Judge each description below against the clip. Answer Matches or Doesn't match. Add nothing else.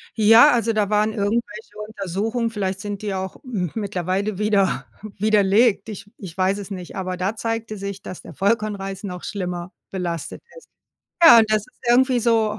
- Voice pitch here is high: Matches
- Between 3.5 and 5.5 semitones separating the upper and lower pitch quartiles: Doesn't match